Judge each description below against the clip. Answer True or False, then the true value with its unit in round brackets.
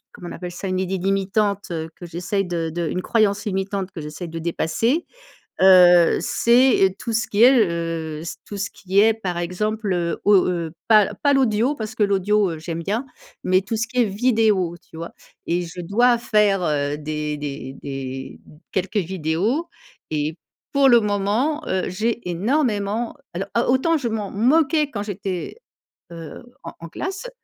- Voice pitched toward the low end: False (195 Hz)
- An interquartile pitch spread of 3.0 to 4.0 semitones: False (4.7 semitones)